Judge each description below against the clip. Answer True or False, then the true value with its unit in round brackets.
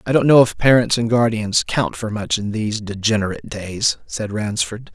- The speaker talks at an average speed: True (195 wpm)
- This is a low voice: True (110 Hz)